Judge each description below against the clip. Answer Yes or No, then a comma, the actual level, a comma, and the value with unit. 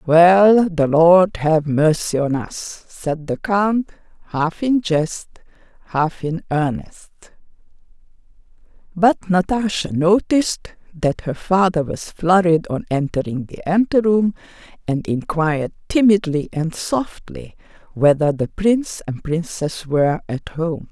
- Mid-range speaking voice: Yes, medium, 170 Hz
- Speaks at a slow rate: Yes, slow, 120 wpm